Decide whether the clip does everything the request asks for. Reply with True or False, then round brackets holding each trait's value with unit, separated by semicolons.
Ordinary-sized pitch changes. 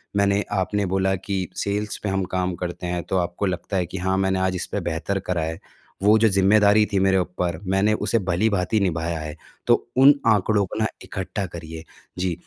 False (2.2 semitones)